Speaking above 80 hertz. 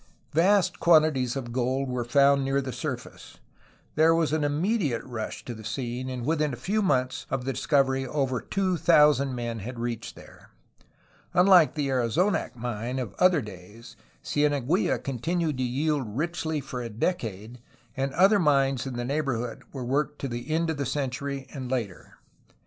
Yes: low, 135 Hz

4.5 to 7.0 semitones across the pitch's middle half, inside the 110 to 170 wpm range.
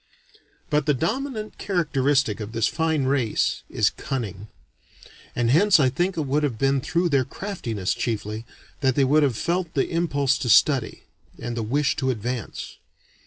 Yes: average, 5.0 semitones; average, 165 wpm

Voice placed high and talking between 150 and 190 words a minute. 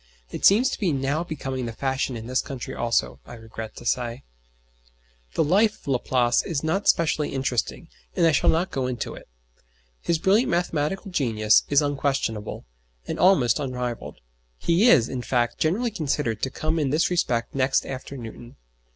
No: low, 135 Hz; average, 170 wpm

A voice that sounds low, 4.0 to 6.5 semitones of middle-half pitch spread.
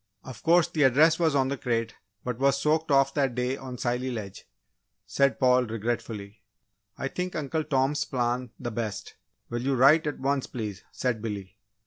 No: low, 130 Hz; average, 2.9 semitones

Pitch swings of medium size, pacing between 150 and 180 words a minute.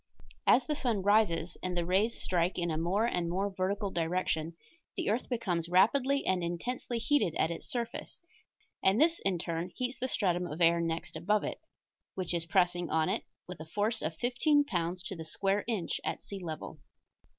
No: average, 4.6 semitones; average, 190 wpm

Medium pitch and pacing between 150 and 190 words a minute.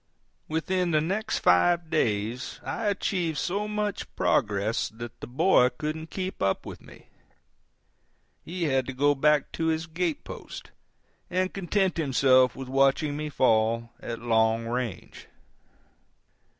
No: medium, 150 Hz; slow, 135 wpm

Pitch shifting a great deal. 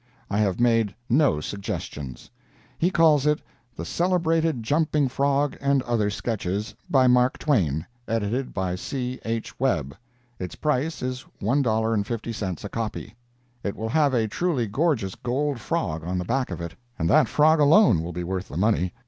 Yes: wide, 6.3 semitones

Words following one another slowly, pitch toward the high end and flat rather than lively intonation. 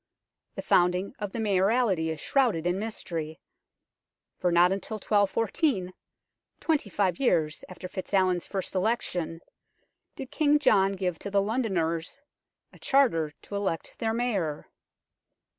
No: slow, 125 wpm; high, 195 Hz; average, 4.1 semitones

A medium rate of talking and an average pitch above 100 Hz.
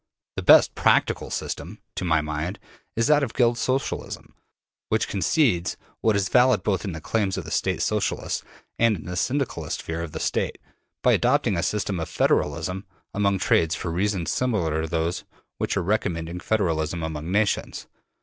No: average, 170 wpm; very low, 95 Hz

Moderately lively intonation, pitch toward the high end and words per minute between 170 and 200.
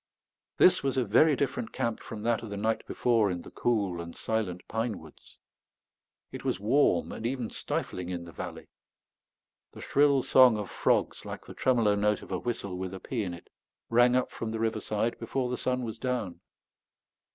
No: average, 3.7 semitones; low, 110 Hz; average, 190 wpm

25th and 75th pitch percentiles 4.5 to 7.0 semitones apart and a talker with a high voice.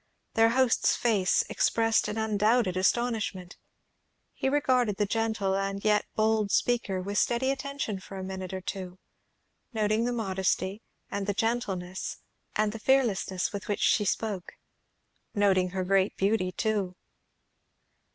No: average, 2.9 semitones; high, 210 Hz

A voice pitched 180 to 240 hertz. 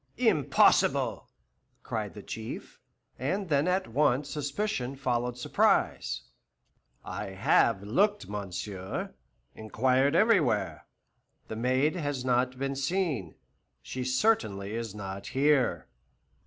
No: low, 130 Hz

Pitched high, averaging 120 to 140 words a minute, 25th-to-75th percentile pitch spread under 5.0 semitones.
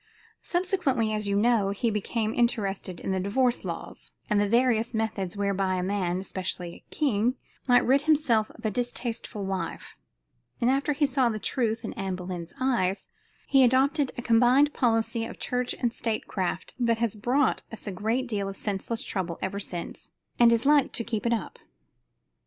No: high, 225 Hz; average, 175 wpm; average, 3.9 semitones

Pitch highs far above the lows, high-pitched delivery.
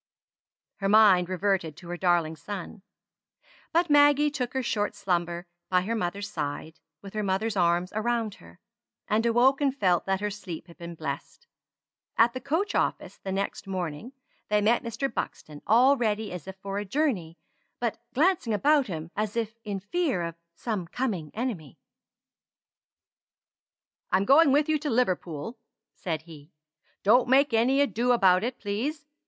Yes: wide, 5.8 semitones; high, 210 Hz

